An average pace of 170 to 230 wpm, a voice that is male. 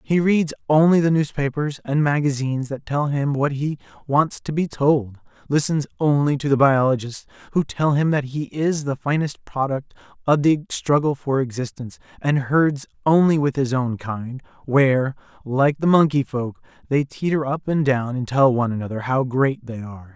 Yes: average, 180 wpm; male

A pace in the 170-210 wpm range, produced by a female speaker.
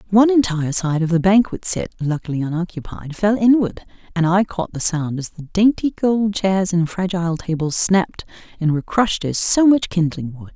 Yes: average, 190 wpm; female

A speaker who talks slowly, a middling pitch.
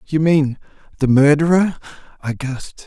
Yes: slow, 105 wpm; medium, 145 Hz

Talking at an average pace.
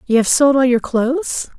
No: fast, 225 wpm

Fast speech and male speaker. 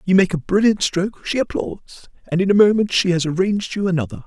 Yes: fast, 225 wpm; male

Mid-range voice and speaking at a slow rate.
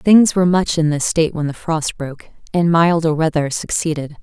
No: medium, 160 Hz; average, 200 wpm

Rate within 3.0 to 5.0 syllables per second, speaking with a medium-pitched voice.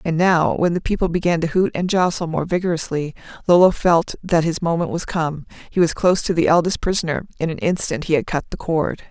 No: 5.8 syllables/s; medium, 165 Hz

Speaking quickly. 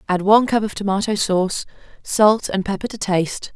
No: average, 185 wpm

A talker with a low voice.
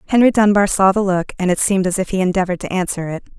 No: high, 190 Hz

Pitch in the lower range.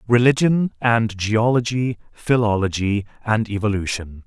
Yes: low, 110 Hz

